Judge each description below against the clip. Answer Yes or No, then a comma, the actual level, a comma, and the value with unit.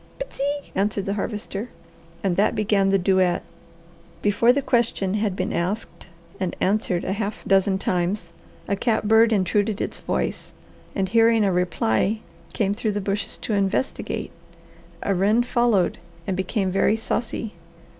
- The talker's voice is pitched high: Yes, high, 205 Hz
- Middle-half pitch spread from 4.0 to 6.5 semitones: No, average, 2.7 semitones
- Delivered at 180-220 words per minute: No, average, 140 wpm